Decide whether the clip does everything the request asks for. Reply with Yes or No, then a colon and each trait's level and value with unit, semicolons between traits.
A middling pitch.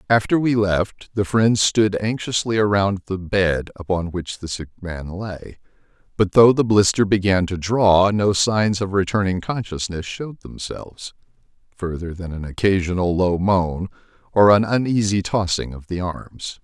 No: very low, 95 Hz